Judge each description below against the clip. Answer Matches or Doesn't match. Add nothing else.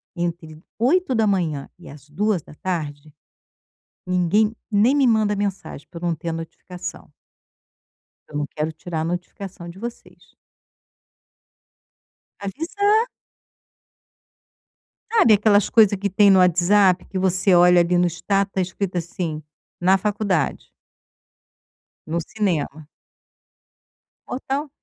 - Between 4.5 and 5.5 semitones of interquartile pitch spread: Doesn't match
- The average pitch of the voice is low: Doesn't match